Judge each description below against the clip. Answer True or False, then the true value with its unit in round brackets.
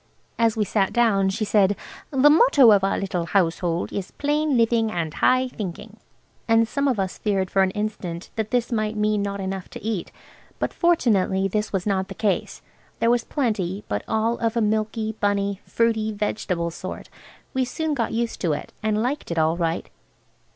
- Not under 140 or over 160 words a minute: False (185 wpm)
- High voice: True (210 Hz)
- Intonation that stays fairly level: False (3.2 semitones)